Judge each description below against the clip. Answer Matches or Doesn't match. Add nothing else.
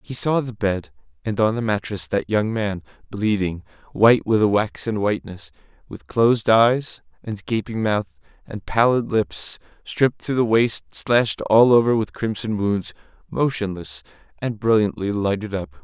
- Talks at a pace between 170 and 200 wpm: Doesn't match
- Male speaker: Matches